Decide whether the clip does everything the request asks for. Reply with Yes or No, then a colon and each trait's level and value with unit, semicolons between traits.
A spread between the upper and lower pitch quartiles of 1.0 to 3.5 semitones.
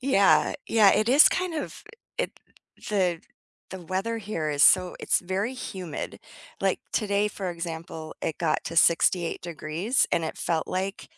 No: average, 4.2 semitones